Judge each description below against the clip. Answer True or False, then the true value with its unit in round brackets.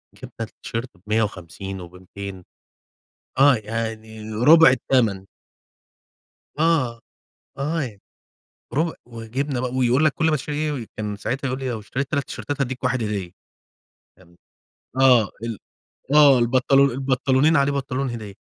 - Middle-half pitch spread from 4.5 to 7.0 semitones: False (4.1 semitones)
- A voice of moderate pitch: False (125 Hz)